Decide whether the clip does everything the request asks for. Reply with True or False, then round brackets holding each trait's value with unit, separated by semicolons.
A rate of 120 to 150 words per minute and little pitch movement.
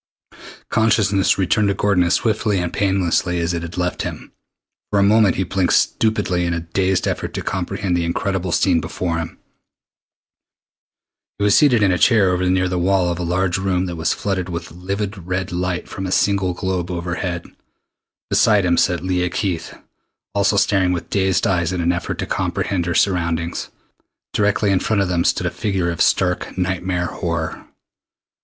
False (180 wpm; 2.0 semitones)